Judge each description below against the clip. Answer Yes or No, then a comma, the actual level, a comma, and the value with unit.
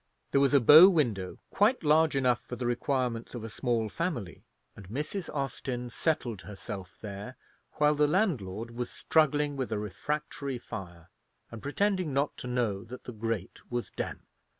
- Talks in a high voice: No, low, 125 Hz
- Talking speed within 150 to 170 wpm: Yes, average, 165 wpm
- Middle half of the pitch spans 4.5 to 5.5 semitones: Yes, average, 5.1 semitones